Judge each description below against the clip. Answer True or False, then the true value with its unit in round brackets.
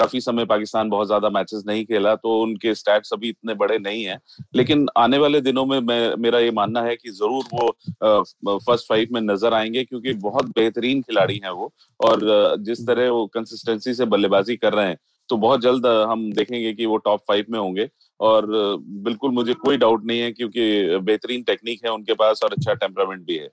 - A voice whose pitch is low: True (115 Hz)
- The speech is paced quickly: True (205 wpm)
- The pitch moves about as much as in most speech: False (2.1 semitones)